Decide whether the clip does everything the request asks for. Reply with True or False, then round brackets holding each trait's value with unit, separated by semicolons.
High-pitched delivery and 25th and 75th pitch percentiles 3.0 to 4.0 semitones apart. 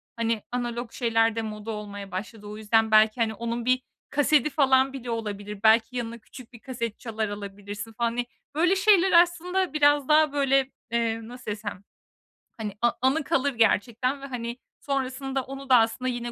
True (235 Hz; 3.4 semitones)